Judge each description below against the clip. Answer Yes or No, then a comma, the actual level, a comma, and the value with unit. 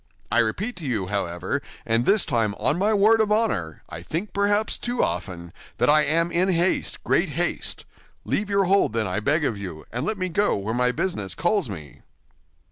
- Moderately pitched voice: Yes, medium, 150 Hz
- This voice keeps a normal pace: Yes, average, 190 wpm